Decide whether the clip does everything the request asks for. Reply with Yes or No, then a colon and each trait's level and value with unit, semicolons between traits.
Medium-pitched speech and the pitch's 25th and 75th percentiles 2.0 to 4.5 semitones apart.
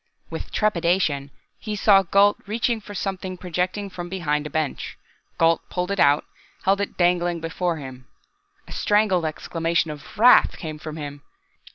Yes: medium, 175 Hz; average, 4.0 semitones